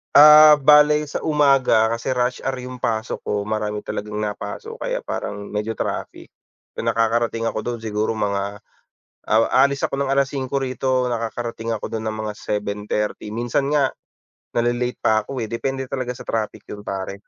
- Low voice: Yes, low, 115 Hz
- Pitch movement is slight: No, average, 4.0 semitones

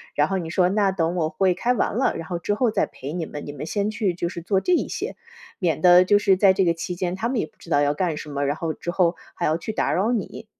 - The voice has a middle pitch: Yes, medium, 180 Hz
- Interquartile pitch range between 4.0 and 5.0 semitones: No, average, 3.5 semitones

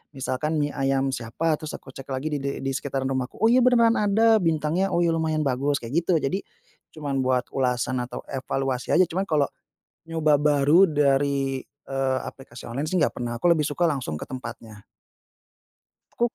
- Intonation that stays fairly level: No, average, 3.7 semitones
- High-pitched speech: No, medium, 140 Hz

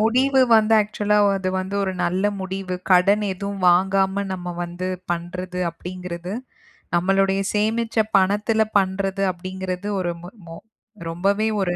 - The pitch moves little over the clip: Yes, narrow, 2.1 semitones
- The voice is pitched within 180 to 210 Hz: Yes, high, 190 Hz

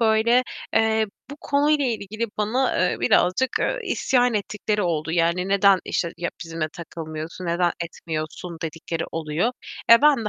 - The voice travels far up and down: Yes, wide, 5.7 semitones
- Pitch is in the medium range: No, high, 195 Hz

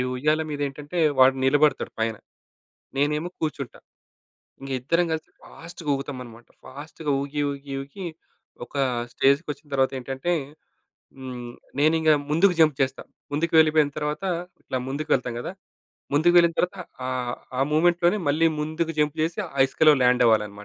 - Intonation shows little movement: No, average, 3.2 semitones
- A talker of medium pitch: Yes, medium, 145 Hz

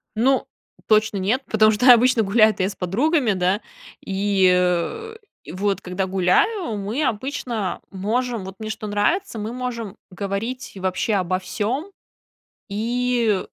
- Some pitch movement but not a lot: Yes, average, 4.4 semitones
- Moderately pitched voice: No, high, 215 Hz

